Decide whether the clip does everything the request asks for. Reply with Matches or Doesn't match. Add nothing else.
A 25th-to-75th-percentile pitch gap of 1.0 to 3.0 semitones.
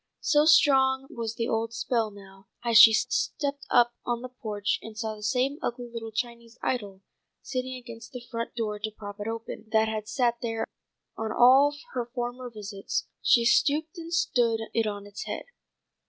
Matches